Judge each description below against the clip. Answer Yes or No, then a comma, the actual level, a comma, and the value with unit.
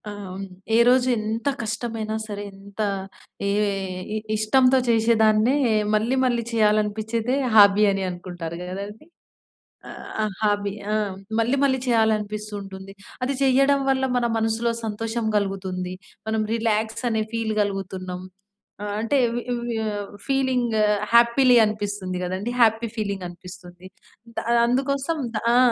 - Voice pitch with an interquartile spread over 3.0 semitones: No, average, 2.7 semitones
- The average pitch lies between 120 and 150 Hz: No, high, 220 Hz